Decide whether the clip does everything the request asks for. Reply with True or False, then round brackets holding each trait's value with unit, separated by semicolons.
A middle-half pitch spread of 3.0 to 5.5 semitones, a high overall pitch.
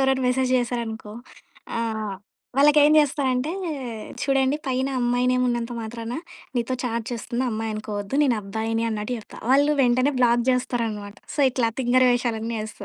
False (2.5 semitones; 240 Hz)